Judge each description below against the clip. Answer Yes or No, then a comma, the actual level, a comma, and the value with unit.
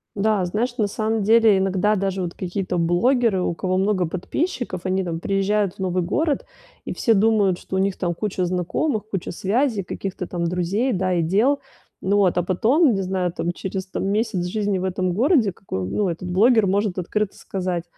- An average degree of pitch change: Yes, average, 3.0 semitones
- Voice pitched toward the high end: Yes, high, 195 Hz